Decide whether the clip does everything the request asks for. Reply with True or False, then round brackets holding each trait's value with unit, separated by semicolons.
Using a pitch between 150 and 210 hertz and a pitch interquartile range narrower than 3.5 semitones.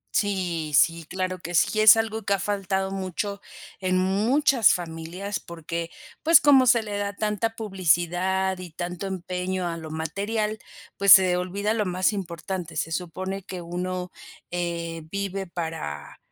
True (185 Hz; 2.7 semitones)